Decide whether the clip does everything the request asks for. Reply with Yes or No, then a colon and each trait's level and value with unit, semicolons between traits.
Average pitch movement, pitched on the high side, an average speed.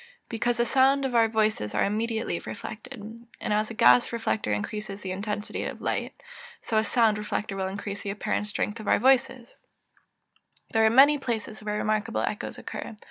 No: narrow, 2.1 semitones; high, 215 Hz; average, 185 wpm